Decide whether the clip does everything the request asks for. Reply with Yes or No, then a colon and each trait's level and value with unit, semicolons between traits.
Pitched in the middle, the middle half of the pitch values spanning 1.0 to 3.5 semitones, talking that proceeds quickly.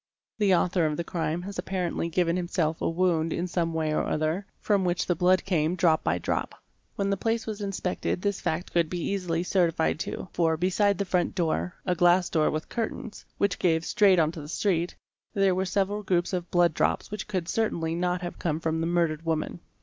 Yes: medium, 175 Hz; narrow, 2.5 semitones; fast, 210 wpm